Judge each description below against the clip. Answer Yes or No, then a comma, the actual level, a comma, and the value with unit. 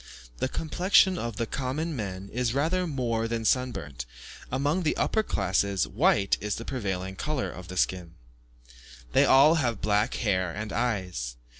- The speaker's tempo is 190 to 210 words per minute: No, average, 155 wpm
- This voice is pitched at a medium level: No, low, 115 Hz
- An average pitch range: No, wide, 6.2 semitones